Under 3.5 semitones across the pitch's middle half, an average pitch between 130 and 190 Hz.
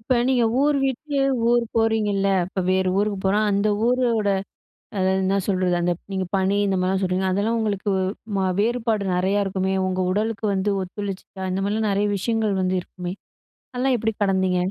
No: average, 2.8 semitones; high, 200 Hz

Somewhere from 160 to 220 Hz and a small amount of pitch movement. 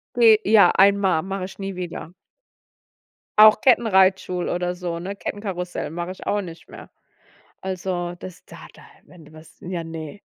Yes: medium, 185 Hz; narrow, 2.2 semitones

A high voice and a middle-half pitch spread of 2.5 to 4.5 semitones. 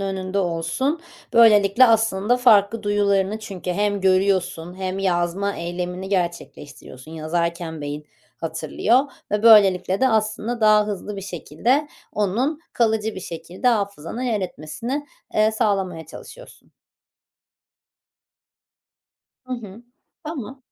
Yes: high, 200 Hz; average, 3.9 semitones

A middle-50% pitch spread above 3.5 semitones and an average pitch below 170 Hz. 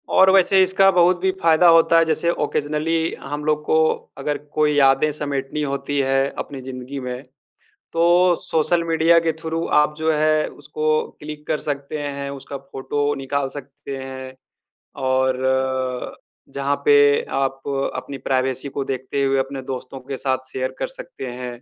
No: average, 2.7 semitones; medium, 140 Hz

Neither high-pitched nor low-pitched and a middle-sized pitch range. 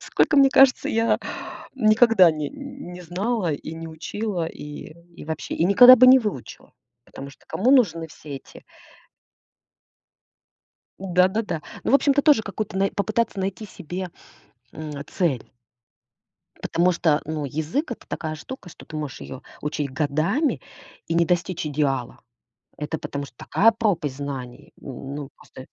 No: medium, 170 Hz; wide, 6.4 semitones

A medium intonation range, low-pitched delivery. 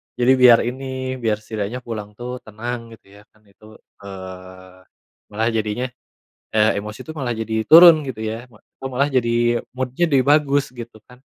Yes: average, 3.3 semitones; low, 120 Hz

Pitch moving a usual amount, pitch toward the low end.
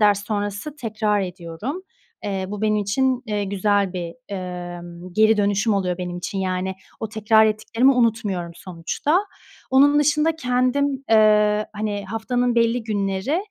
No: average, 3.9 semitones; high, 210 Hz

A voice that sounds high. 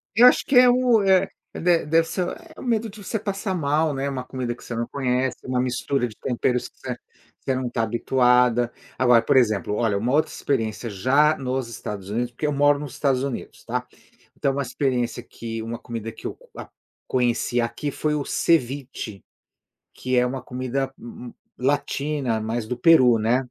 No: low, 130 Hz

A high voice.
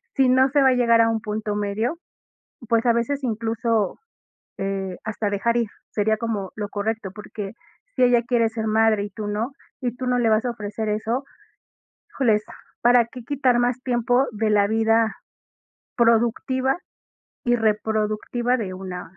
Yes: high, 225 Hz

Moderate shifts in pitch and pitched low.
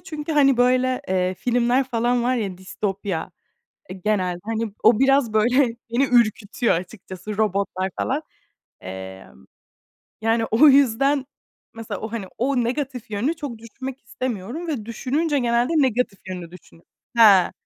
No: average, 4.5 semitones; high, 230 Hz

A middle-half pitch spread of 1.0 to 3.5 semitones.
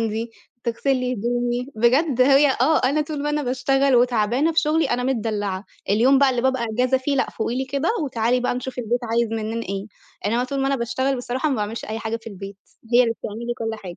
Yes: average, 3.0 semitones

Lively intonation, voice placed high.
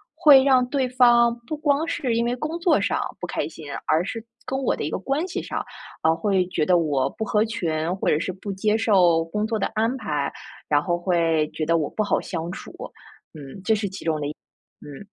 Yes: wide, 6.7 semitones; high, 195 Hz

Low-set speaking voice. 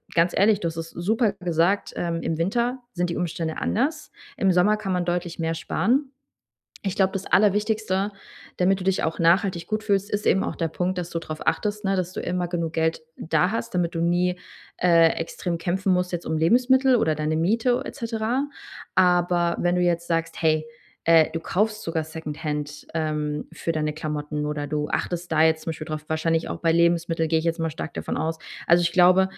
No: medium, 175 Hz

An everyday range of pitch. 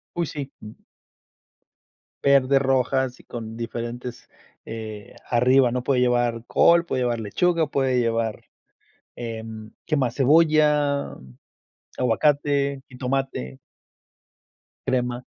Yes: average, 3.1 semitones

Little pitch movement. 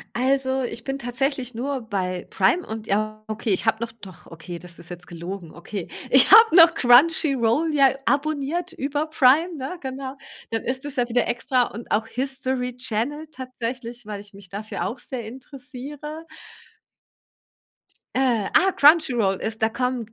No: average, 4.1 semitones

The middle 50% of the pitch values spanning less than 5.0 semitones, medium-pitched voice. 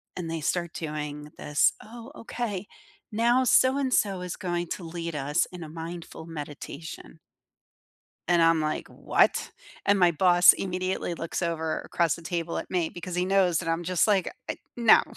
Yes: narrow, 2.5 semitones; medium, 175 Hz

